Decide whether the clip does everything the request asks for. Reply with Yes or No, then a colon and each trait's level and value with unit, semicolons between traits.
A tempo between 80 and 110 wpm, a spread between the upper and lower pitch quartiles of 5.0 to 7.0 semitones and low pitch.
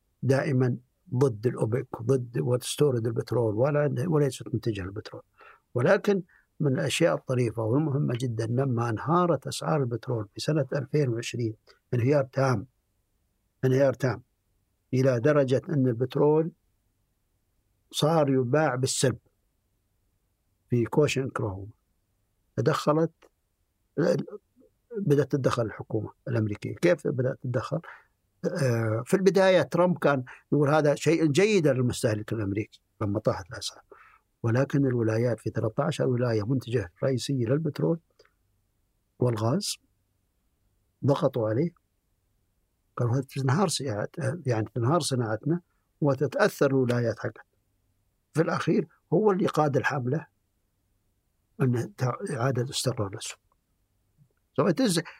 Yes: average, 95 wpm; average, 5.3 semitones; low, 125 Hz